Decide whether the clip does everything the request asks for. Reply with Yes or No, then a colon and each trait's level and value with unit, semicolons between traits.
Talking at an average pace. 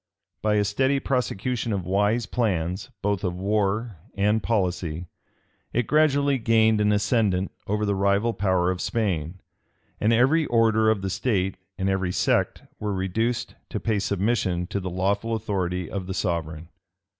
Yes: average, 155 wpm